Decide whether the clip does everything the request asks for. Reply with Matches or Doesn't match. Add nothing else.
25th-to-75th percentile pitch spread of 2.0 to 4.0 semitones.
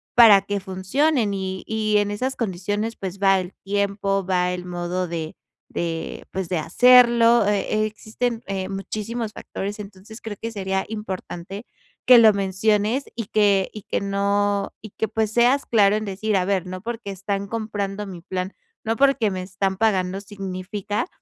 Matches